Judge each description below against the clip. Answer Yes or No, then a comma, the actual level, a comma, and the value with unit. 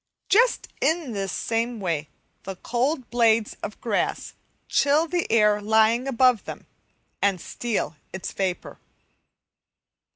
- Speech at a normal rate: No, slow, 120 wpm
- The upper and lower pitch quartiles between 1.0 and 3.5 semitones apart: No, average, 4.1 semitones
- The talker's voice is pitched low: No, high, 230 Hz